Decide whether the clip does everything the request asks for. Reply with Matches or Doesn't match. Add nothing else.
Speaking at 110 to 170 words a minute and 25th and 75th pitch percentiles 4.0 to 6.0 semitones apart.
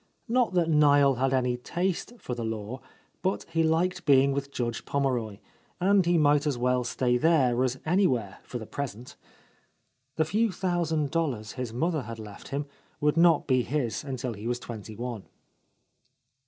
Matches